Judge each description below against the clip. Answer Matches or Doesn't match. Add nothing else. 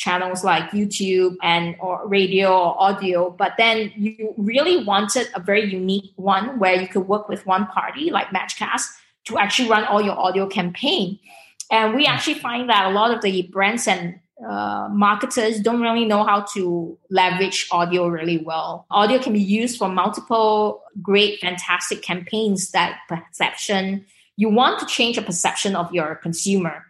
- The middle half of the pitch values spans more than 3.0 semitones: Doesn't match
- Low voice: Doesn't match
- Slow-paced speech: Doesn't match